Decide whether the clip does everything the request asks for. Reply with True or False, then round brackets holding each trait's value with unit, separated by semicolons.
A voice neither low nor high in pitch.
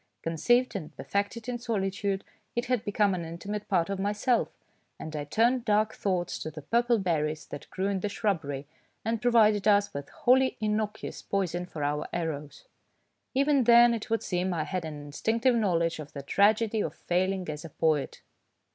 False (200 Hz)